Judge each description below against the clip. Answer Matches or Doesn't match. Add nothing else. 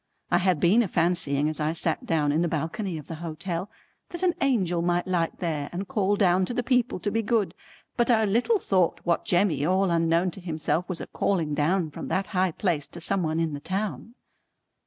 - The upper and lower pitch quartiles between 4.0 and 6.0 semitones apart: Doesn't match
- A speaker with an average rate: Doesn't match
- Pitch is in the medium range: Matches